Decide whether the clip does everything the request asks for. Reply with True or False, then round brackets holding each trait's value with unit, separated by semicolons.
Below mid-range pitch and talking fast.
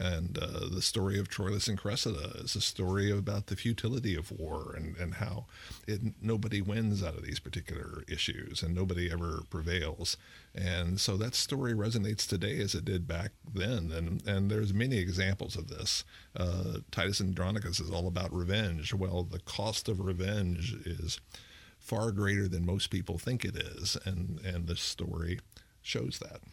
False (95 Hz; 170 wpm)